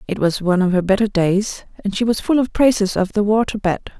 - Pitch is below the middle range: No, high, 205 Hz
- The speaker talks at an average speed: No, fast, 255 wpm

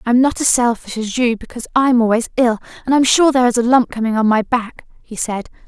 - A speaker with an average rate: No, fast, 245 wpm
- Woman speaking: Yes, female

